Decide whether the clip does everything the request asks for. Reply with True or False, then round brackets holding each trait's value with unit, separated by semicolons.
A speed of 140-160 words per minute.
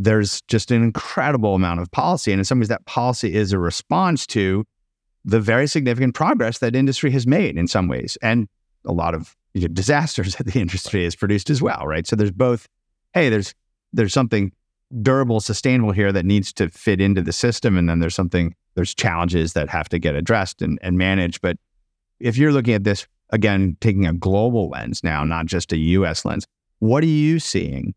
False (205 wpm)